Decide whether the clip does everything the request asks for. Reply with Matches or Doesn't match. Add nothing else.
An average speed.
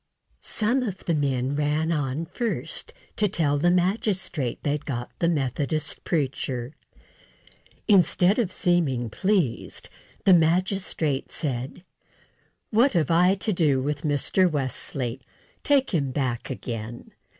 Doesn't match